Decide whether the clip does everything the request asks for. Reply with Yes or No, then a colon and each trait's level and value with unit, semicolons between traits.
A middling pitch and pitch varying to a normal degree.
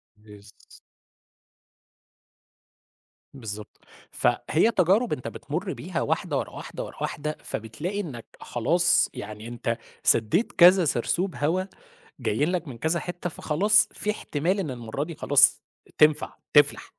No: medium, 150 Hz; wide, 7.1 semitones